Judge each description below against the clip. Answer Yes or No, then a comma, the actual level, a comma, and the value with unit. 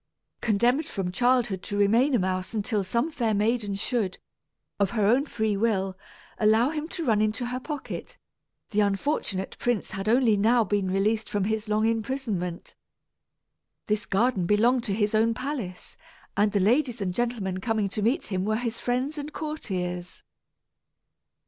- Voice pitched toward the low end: No, high, 215 Hz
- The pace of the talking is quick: No, average, 160 wpm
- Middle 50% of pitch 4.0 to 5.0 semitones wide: No, average, 3.6 semitones